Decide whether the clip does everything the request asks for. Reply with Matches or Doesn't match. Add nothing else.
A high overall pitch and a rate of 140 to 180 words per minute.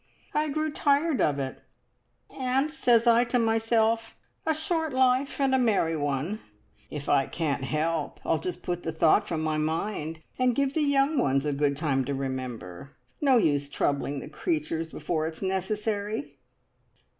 Doesn't match